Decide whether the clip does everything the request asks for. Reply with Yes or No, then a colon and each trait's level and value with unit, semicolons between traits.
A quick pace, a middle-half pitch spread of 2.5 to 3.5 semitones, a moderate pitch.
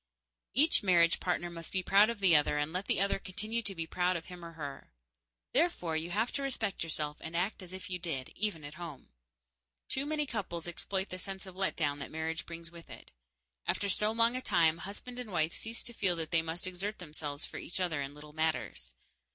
No: fast, 225 wpm; average, 3.9 semitones; medium, 175 Hz